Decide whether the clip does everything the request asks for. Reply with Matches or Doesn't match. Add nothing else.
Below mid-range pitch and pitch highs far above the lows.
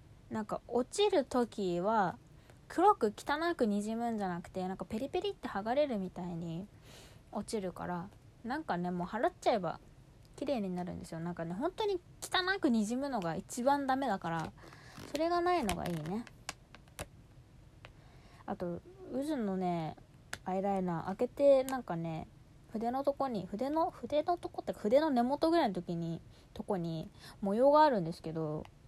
Doesn't match